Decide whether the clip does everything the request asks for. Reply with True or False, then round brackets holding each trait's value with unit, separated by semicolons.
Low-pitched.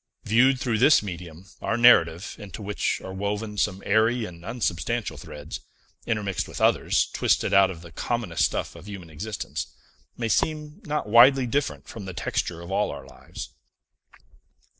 True (105 Hz)